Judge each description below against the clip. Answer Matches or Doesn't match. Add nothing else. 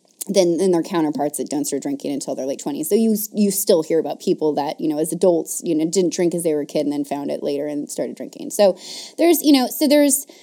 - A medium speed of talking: Doesn't match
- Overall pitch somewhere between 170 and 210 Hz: Matches